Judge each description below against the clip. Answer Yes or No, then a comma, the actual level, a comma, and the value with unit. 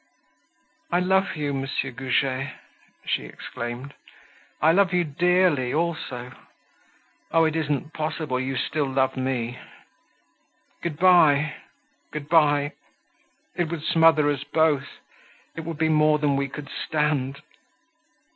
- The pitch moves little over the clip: No, average, 3.2 semitones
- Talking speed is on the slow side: Yes, slow, 120 wpm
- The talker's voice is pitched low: No, medium, 150 Hz